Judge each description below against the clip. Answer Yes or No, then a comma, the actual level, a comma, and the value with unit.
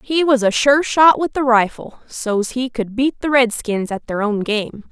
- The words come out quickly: Yes, fast, 220 wpm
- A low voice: No, high, 245 Hz